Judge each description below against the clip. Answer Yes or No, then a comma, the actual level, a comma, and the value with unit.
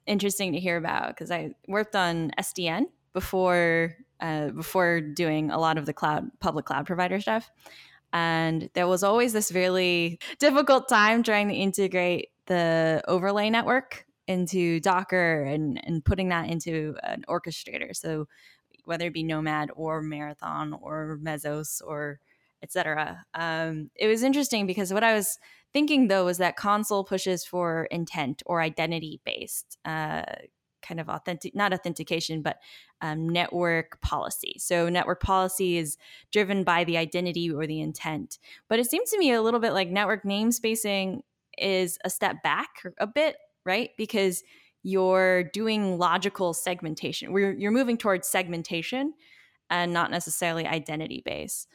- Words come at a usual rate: Yes, average, 150 wpm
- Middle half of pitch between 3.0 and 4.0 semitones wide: Yes, average, 3.7 semitones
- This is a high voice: No, medium, 180 Hz